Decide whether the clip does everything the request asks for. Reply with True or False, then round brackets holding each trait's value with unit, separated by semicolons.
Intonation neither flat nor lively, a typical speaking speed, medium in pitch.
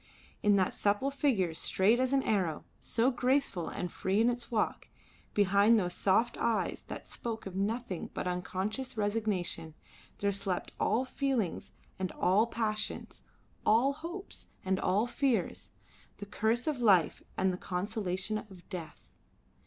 False (4.2 semitones; 145 wpm; 210 Hz)